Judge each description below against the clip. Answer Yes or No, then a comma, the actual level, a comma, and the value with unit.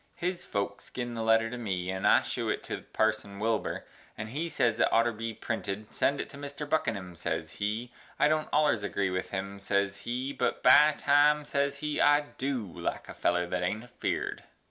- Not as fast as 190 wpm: No, fast, 205 wpm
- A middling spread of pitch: No, wide, 5.9 semitones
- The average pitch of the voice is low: Yes, low, 115 Hz